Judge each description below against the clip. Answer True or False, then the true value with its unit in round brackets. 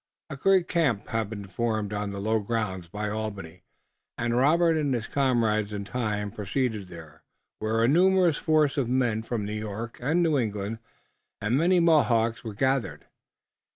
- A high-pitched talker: False (115 Hz)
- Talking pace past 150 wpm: True (165 wpm)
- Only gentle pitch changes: False (4.7 semitones)